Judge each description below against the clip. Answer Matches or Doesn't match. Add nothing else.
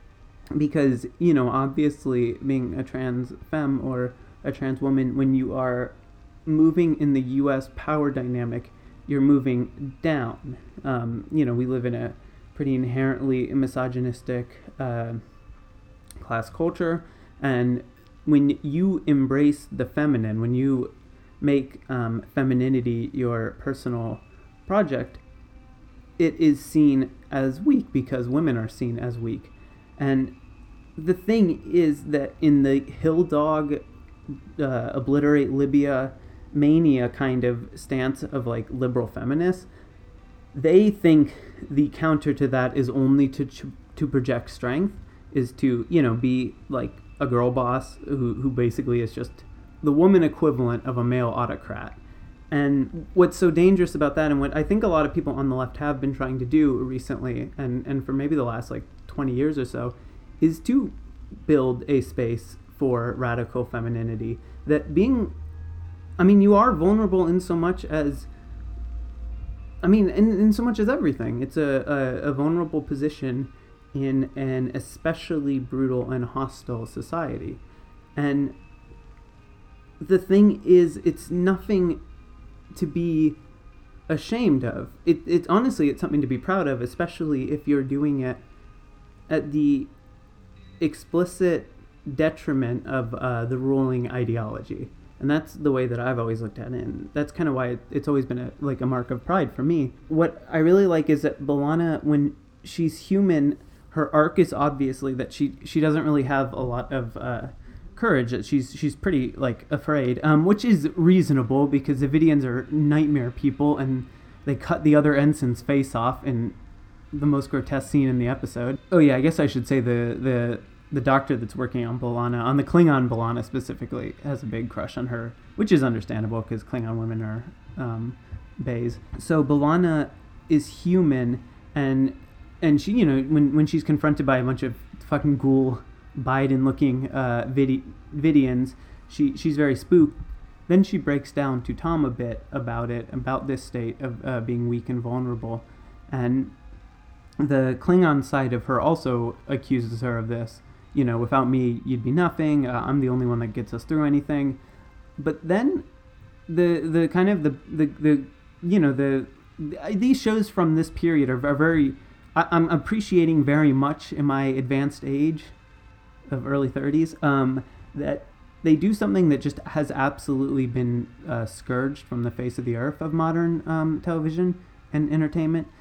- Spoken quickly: Doesn't match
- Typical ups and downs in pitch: Matches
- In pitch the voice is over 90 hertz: Matches